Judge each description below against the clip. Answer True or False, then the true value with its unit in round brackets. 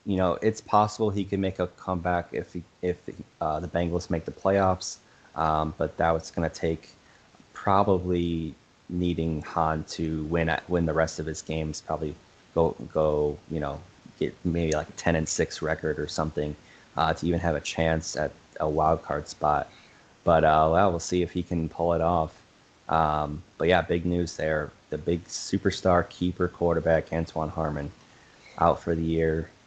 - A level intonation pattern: True (2.1 semitones)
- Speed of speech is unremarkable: True (180 wpm)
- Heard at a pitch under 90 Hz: True (80 Hz)